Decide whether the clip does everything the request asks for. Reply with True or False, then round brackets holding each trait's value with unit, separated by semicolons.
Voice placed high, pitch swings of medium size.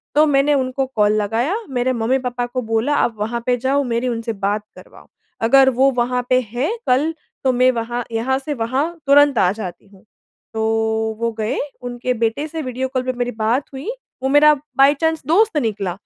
True (250 Hz; 3.1 semitones)